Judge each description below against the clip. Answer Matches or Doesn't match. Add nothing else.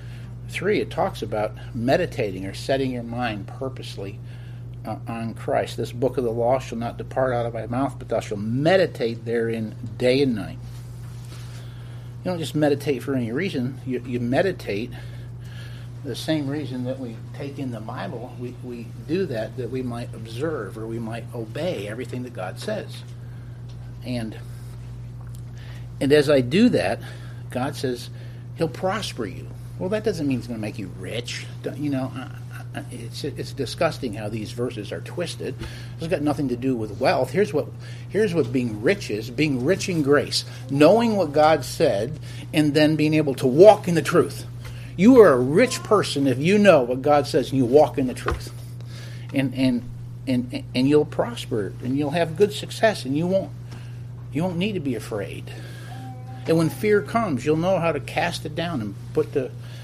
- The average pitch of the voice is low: Matches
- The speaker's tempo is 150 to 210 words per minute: Matches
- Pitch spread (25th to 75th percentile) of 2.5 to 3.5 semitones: Matches